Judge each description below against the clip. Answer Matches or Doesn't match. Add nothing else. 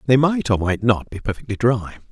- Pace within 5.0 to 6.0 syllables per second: Matches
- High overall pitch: Doesn't match